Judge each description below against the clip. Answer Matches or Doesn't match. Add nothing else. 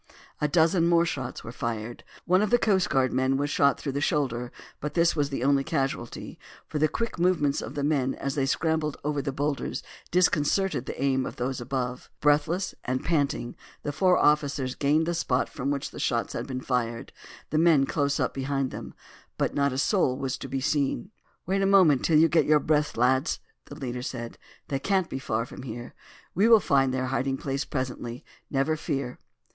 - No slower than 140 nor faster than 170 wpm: Doesn't match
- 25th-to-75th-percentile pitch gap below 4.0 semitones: Matches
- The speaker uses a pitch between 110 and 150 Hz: Matches